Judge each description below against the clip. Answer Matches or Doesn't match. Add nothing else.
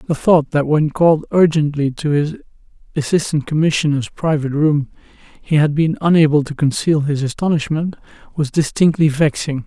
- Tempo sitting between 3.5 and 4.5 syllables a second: Doesn't match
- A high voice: Doesn't match